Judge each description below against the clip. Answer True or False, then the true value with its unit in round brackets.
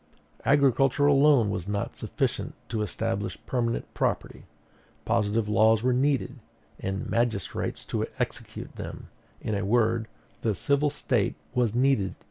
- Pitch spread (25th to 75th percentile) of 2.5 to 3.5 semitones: False (4.3 semitones)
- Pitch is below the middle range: True (115 Hz)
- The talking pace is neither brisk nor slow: False (125 wpm)